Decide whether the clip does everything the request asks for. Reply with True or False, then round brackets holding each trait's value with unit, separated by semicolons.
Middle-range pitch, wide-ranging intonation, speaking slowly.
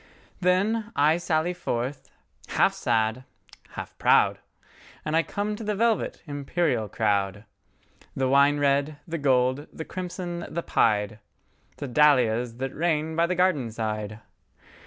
True (145 Hz; 6.5 semitones; 120 wpm)